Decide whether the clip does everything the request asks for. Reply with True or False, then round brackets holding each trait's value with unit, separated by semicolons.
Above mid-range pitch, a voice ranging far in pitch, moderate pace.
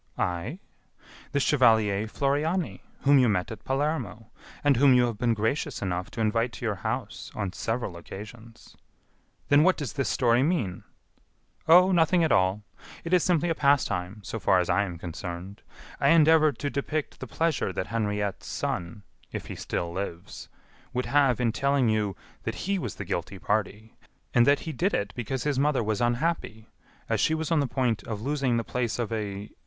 False (120 Hz; 5.8 semitones; 185 wpm)